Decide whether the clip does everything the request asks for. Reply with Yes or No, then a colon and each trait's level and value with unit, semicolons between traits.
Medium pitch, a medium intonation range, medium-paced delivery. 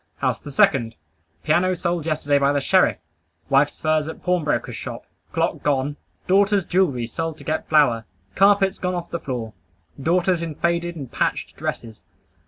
Yes: medium, 160 Hz; average, 4.0 semitones; average, 160 wpm